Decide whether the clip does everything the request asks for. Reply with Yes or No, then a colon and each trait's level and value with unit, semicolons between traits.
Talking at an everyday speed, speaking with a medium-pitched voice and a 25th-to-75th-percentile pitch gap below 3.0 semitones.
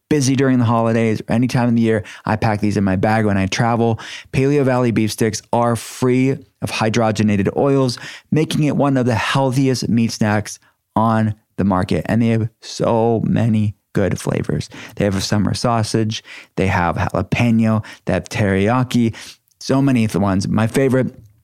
No: average, 180 wpm; low, 115 Hz; narrow, 2.6 semitones